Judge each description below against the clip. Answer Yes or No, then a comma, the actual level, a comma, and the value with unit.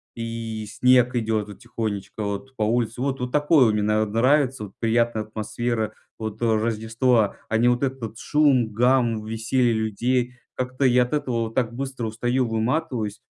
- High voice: No, low, 115 Hz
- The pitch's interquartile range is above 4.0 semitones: No, narrow, 2.4 semitones